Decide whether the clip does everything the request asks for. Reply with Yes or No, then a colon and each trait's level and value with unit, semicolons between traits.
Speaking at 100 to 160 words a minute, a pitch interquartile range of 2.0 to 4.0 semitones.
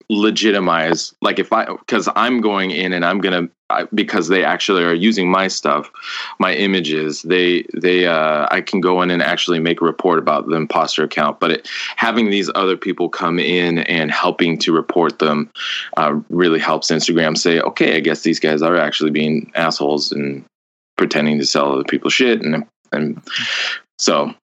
No: average, 180 wpm; average, 3.6 semitones